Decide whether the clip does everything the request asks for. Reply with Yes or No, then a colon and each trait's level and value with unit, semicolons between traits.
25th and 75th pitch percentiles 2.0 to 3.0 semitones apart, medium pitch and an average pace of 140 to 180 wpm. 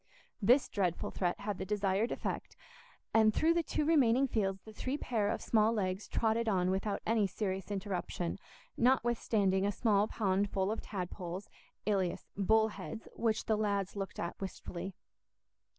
No: average, 2.7 semitones; high, 205 Hz; average, 150 wpm